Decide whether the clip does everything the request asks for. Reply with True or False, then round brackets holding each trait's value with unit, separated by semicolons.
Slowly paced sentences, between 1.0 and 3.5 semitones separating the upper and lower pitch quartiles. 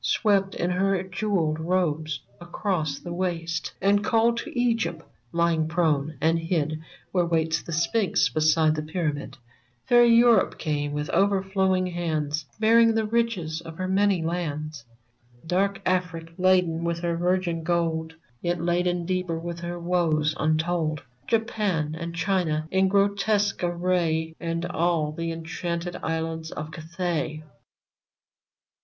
True (130 wpm; 2.7 semitones)